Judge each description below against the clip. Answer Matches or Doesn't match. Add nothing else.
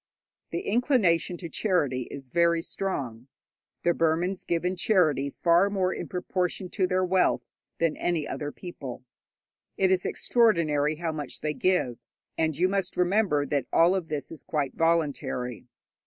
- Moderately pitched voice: Matches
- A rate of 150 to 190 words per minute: Matches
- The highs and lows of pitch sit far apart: Doesn't match